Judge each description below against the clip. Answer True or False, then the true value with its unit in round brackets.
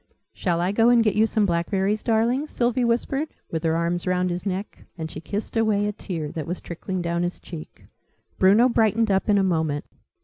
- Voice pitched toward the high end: True (195 Hz)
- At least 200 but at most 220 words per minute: True (205 wpm)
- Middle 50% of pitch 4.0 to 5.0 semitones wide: True (4.6 semitones)